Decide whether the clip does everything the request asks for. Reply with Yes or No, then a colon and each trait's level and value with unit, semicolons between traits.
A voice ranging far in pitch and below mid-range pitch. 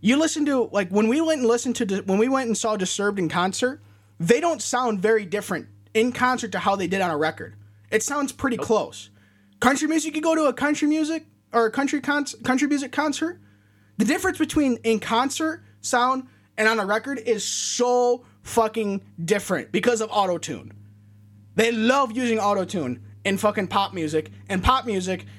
No: wide, 6.1 semitones; high, 220 Hz